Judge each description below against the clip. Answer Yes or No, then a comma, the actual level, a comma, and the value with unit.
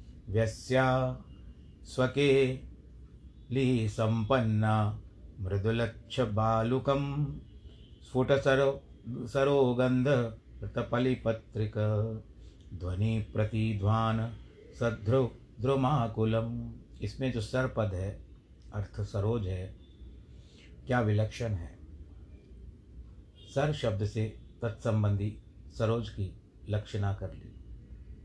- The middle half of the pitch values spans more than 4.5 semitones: No, average, 3.4 semitones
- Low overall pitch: Yes, low, 110 Hz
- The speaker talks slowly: Yes, slow, 65 wpm